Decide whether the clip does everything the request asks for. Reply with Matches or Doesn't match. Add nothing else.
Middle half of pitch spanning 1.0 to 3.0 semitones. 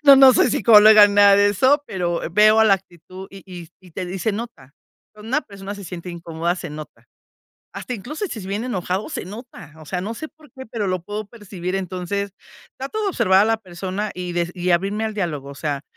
Doesn't match